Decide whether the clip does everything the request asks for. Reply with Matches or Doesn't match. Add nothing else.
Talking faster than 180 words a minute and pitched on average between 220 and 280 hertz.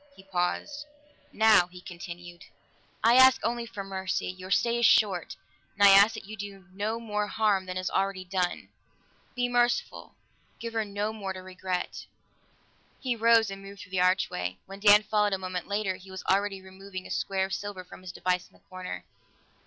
Doesn't match